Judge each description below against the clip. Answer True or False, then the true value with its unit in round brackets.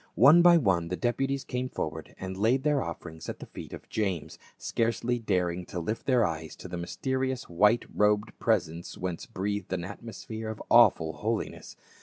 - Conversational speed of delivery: True (175 wpm)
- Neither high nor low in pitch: False (105 Hz)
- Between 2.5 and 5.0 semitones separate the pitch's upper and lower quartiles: False (5.4 semitones)